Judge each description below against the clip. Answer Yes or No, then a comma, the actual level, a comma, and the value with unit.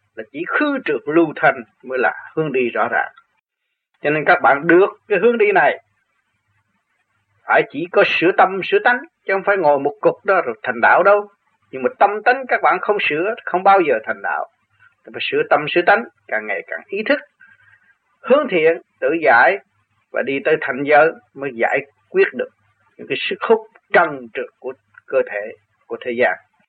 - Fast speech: No, average, 195 wpm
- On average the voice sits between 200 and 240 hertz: No, very high, 250 Hz